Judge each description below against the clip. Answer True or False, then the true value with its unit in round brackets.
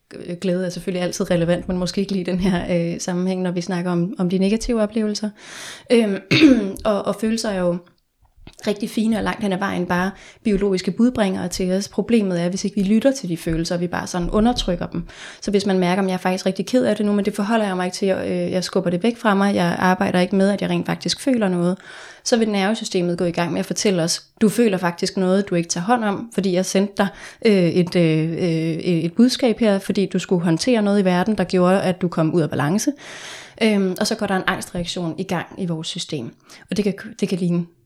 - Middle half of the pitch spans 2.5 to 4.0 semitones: True (2.8 semitones)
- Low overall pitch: False (190 Hz)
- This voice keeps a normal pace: False (240 wpm)